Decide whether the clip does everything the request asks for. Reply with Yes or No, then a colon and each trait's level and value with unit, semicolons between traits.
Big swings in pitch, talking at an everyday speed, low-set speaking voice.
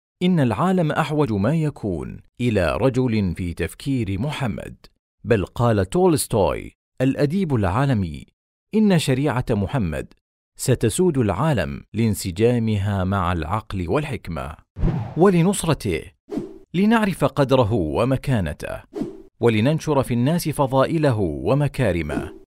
Yes: wide, 6.9 semitones; average, 90 wpm; low, 125 Hz